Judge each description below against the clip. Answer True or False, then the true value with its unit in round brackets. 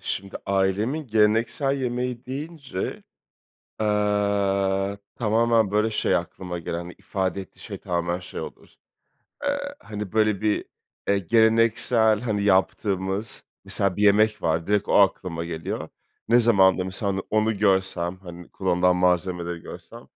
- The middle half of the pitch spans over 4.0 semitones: False (3.0 semitones)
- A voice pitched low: True (100 Hz)